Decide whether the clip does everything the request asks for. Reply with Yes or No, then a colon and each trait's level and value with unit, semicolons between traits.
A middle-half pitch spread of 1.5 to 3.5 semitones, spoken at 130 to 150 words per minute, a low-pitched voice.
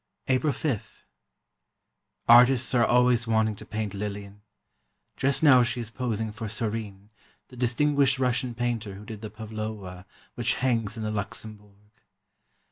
Yes: average, 2.8 semitones; slow, 135 wpm; low, 110 Hz